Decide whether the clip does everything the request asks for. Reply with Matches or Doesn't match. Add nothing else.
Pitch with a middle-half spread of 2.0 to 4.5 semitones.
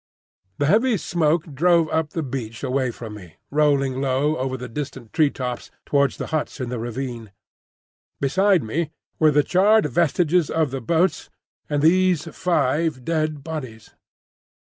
Matches